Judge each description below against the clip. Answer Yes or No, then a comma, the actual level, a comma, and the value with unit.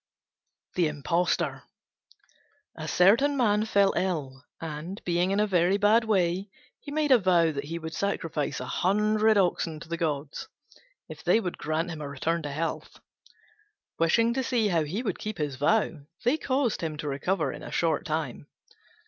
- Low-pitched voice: No, medium, 175 Hz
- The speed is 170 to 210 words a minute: Yes, average, 175 wpm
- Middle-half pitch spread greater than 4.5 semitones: Yes, average, 5.1 semitones